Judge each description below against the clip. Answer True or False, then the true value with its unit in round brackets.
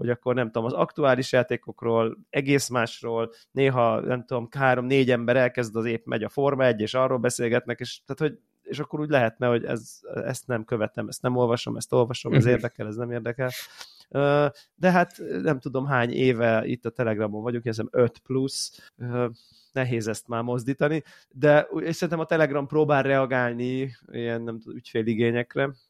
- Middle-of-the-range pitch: False (125 Hz)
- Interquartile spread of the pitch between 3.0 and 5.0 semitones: False (2.6 semitones)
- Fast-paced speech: True (170 wpm)